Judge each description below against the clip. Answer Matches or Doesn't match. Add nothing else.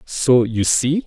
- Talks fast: Doesn't match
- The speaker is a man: Matches